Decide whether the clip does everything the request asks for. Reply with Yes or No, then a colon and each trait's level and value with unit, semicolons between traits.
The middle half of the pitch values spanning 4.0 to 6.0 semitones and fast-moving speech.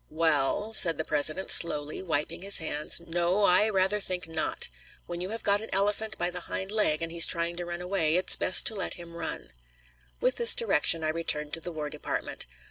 No: average, 3.4 semitones; fast, 210 wpm